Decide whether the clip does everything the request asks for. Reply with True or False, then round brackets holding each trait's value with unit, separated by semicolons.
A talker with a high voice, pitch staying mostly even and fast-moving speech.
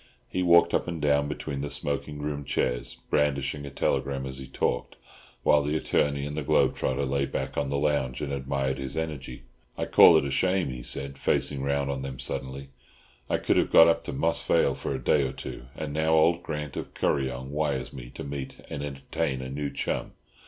False (70 Hz; 1.7 semitones; 210 wpm)